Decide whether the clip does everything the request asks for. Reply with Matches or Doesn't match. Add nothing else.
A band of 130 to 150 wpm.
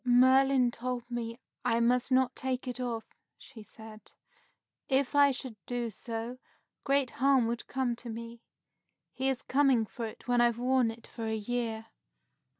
Doesn't match